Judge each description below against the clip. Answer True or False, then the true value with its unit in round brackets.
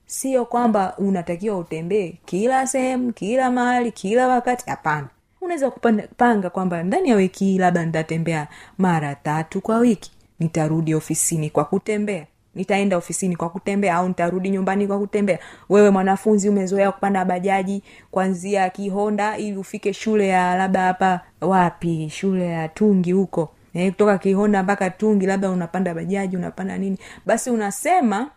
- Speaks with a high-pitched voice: True (195 Hz)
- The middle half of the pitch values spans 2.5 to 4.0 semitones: True (2.8 semitones)